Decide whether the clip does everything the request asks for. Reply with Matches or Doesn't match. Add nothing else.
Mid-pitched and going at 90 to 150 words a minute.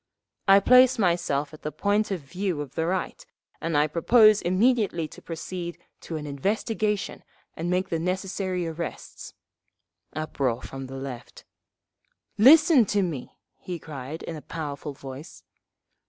Matches